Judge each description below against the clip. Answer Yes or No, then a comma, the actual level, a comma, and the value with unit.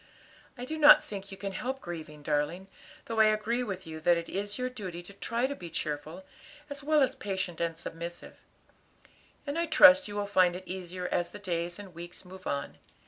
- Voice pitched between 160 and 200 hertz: Yes, high, 190 Hz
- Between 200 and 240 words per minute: Yes, fast, 205 wpm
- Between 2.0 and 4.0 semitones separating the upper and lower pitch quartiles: No, average, 4.8 semitones